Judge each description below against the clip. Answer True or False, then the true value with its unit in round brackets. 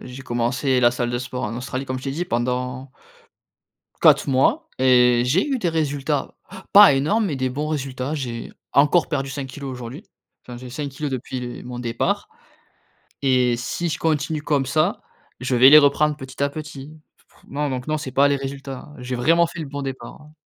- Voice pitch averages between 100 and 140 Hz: True (135 Hz)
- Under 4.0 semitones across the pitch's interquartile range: True (3.0 semitones)